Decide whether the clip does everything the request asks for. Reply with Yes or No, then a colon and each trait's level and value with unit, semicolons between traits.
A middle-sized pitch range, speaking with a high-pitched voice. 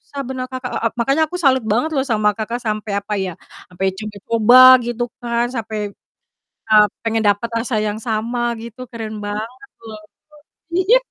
Yes: average, 3.0 semitones; high, 230 Hz